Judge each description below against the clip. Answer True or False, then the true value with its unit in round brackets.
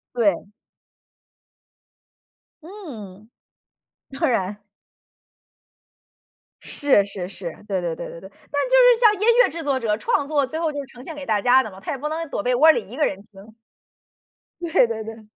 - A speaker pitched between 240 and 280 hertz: True (245 Hz)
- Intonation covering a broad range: True (6.9 semitones)